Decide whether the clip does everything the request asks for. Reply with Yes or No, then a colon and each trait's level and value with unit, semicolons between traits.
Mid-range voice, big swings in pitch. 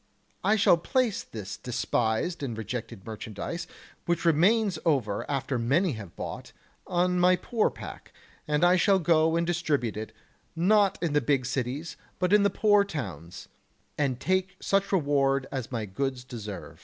Yes: medium, 150 Hz; wide, 6.7 semitones